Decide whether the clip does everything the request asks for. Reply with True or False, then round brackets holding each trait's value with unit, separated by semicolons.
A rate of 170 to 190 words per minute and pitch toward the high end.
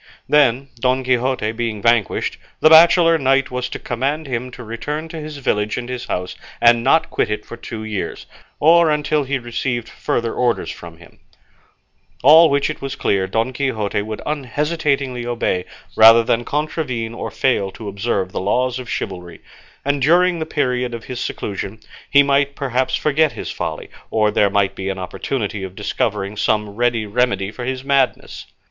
False (175 wpm; 125 Hz)